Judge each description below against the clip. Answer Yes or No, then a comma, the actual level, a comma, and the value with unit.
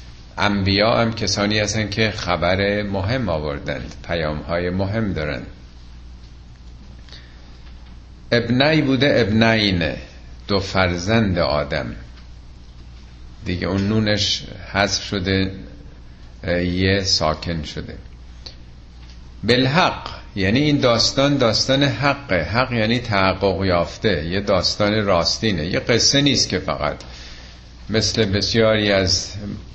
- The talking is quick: No, slow, 95 wpm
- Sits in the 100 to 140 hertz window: No, very low, 90 Hz